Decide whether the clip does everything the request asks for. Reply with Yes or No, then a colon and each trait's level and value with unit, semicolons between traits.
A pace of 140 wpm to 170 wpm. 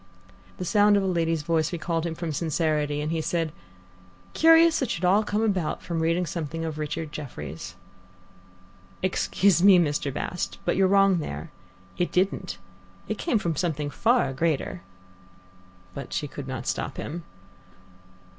Yes: average, 155 wpm